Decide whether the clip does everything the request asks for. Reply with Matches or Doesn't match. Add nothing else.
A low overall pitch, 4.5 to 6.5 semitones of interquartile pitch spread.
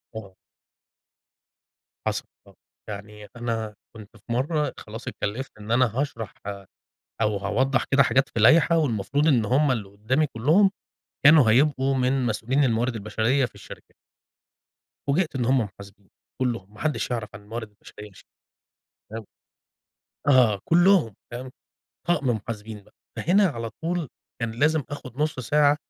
Matches